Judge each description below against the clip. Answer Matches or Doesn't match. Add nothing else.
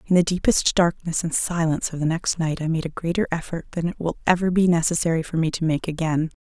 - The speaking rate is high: Matches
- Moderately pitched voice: Matches